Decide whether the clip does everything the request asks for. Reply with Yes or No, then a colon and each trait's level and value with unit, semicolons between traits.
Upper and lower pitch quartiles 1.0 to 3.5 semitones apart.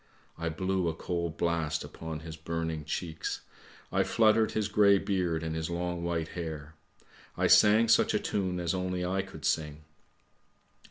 Yes: average, 2.7 semitones